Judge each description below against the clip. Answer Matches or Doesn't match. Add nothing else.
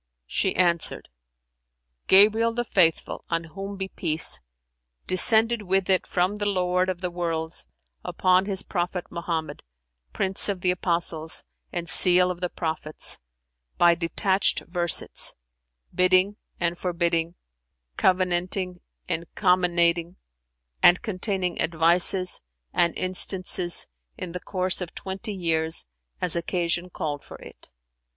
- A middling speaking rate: Doesn't match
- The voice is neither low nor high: Matches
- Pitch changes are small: Matches